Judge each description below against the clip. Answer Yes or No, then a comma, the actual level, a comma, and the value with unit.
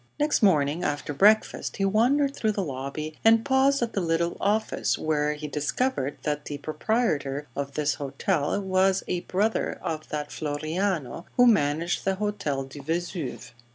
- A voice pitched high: No, medium, 165 Hz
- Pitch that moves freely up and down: Yes, wide, 6.0 semitones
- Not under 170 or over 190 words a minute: No, average, 155 wpm